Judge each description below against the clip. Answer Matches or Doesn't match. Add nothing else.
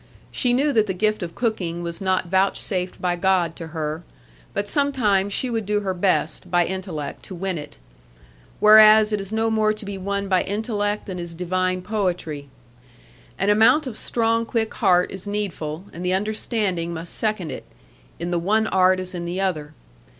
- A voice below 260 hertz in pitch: Matches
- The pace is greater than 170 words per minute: Matches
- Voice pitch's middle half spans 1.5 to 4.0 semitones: Matches